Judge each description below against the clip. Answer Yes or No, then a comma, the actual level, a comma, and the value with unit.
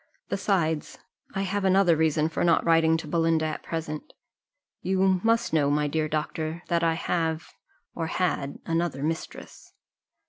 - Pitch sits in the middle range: Yes, medium, 165 Hz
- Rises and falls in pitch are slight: Yes, narrow, 1.8 semitones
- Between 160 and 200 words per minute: No, average, 145 wpm